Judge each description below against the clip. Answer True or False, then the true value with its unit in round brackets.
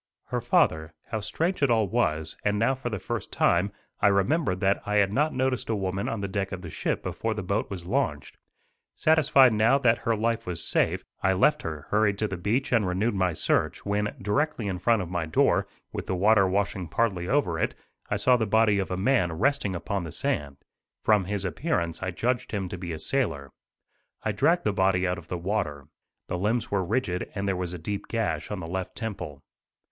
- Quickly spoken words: True (215 wpm)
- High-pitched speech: False (100 Hz)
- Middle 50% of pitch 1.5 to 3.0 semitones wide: False (4.1 semitones)